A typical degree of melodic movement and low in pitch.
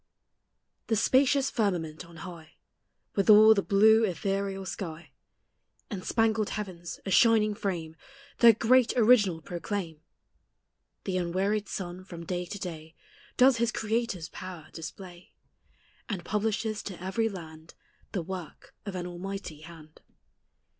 No: average, 4.0 semitones; high, 195 Hz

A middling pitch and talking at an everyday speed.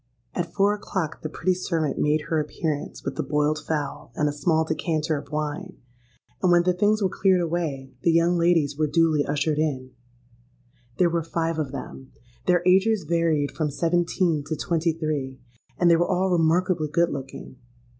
Yes: medium, 160 Hz; average, 175 wpm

